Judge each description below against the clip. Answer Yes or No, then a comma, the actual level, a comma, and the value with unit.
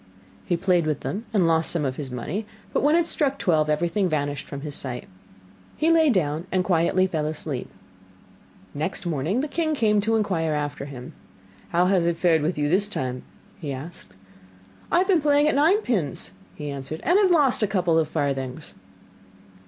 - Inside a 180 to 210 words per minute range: Yes, average, 190 wpm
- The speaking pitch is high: No, medium, 170 Hz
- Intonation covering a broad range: Yes, wide, 6.7 semitones